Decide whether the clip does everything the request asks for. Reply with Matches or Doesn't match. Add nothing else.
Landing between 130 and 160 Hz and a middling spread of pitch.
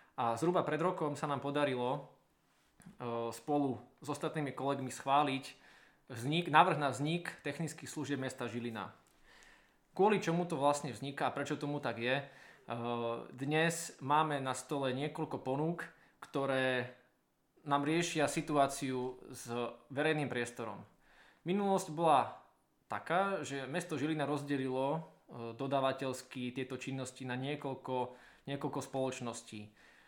Matches